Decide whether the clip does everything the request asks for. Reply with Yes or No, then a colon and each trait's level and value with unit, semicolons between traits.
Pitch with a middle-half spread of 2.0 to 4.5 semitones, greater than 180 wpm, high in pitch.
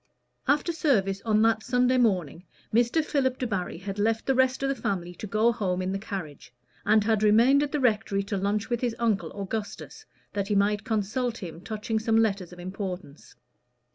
Yes: average, 3.8 semitones; average, 190 wpm; high, 215 Hz